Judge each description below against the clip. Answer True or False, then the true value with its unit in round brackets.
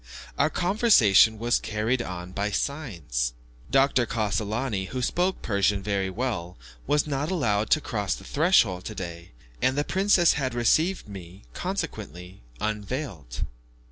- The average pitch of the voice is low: True (110 Hz)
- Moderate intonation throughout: False (6.7 semitones)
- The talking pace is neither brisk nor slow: False (130 wpm)